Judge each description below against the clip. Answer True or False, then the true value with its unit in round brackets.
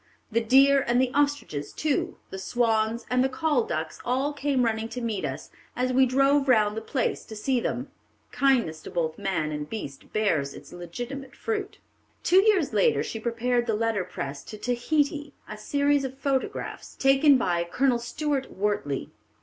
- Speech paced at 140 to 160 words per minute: False (175 wpm)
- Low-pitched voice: False (245 Hz)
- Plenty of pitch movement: False (4.7 semitones)